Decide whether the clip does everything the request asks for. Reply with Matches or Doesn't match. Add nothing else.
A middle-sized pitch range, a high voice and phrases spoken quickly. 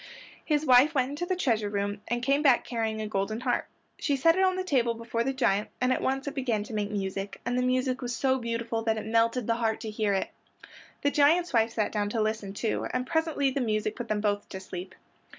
Matches